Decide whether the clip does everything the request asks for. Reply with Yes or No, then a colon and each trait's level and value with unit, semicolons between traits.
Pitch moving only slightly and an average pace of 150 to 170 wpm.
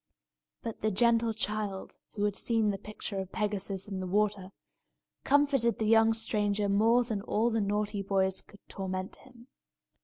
Yes: narrow, 2.3 semitones; average, 160 wpm